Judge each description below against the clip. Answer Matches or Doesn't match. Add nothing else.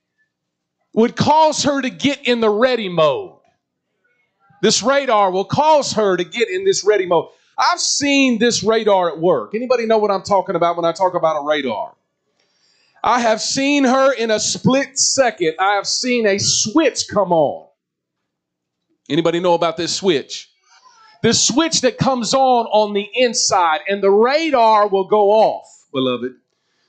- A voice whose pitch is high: Matches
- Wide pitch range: Matches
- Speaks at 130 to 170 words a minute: Matches